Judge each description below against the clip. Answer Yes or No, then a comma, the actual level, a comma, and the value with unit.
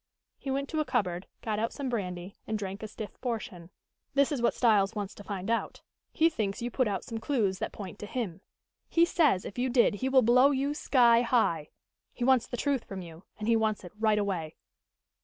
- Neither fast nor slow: No, fast, 220 wpm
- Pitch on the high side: Yes, high, 225 Hz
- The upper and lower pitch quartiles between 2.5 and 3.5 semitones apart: No, average, 4.5 semitones